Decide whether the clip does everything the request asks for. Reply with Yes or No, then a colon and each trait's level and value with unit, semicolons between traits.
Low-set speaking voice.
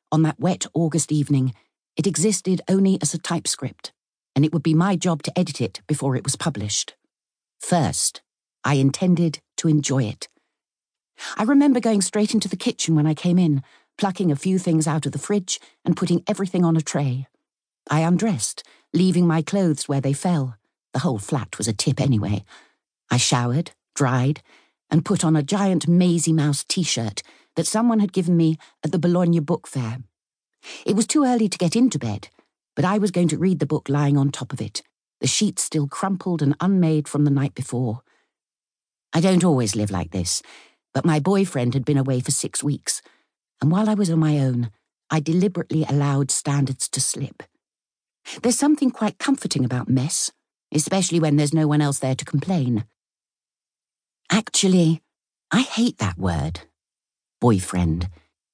No: medium, 155 Hz